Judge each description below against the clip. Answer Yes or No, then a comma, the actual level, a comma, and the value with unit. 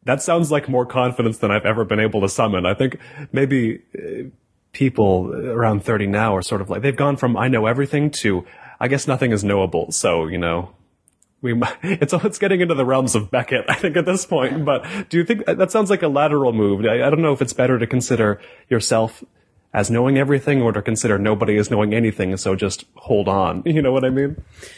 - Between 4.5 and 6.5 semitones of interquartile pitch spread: Yes, average, 5.1 semitones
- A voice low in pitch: Yes, low, 125 Hz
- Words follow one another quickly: Yes, fast, 225 wpm